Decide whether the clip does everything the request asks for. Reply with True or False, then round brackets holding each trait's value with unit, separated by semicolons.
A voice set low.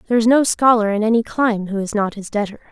False (220 Hz)